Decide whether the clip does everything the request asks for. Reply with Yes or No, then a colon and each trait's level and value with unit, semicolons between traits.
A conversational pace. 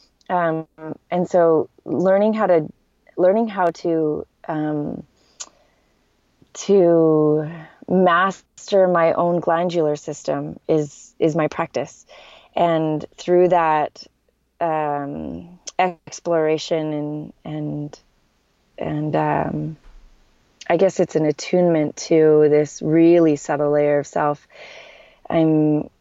No: slow, 95 wpm